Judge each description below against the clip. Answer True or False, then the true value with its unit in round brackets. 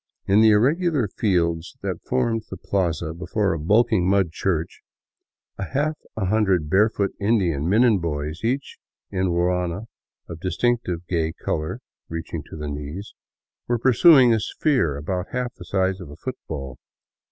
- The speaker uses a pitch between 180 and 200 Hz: False (95 Hz)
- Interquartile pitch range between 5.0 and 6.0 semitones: True (5.3 semitones)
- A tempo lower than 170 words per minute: True (155 wpm)